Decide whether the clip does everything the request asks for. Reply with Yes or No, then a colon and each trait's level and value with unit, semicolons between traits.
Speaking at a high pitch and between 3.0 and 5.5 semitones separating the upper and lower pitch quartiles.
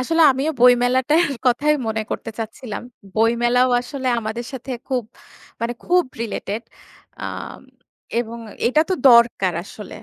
No: high, 245 Hz; narrow, 2.5 semitones